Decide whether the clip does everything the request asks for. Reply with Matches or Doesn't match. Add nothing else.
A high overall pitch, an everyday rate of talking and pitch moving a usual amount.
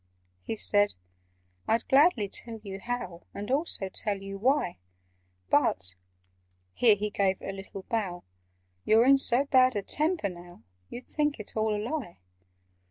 Matches